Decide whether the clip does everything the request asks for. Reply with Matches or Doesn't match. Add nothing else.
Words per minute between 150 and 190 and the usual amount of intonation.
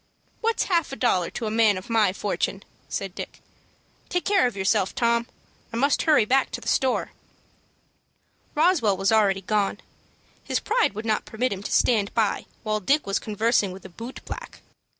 Matches